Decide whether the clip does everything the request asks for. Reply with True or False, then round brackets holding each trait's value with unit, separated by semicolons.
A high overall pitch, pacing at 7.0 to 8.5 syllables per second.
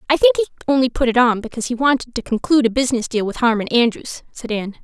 True (250 Hz; 7.2 syllables/s)